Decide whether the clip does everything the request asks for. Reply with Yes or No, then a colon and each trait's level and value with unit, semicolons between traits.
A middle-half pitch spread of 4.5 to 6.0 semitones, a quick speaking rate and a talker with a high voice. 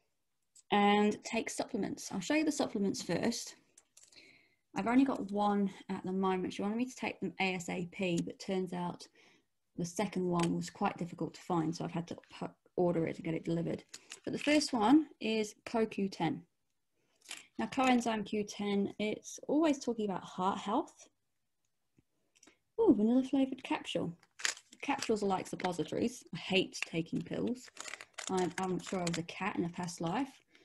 No: average, 5.2 semitones; average, 165 wpm; high, 200 Hz